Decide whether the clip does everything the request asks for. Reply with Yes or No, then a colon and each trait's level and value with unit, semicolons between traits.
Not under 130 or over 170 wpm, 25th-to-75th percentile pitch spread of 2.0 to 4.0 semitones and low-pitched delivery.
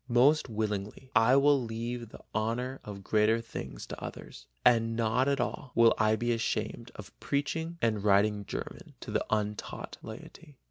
Yes: average, 165 wpm; average, 3.0 semitones; low, 115 Hz